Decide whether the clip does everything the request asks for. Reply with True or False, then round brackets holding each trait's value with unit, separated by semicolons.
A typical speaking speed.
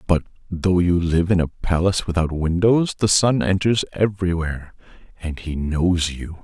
True (160 wpm)